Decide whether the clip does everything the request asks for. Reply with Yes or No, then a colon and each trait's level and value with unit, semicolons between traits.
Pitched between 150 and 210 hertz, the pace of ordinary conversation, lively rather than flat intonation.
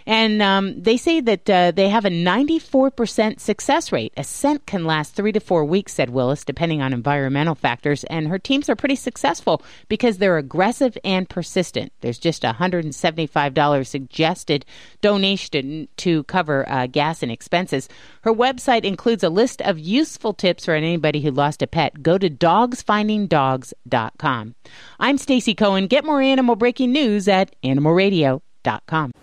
Yes: medium, 185 Hz; average, 155 wpm; wide, 7.0 semitones